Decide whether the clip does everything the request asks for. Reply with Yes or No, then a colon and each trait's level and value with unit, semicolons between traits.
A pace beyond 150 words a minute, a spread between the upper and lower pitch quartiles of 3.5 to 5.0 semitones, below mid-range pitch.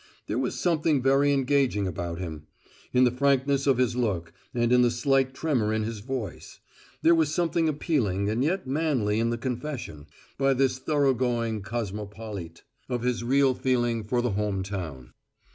Yes: average, 165 wpm; average, 4.5 semitones; low, 125 Hz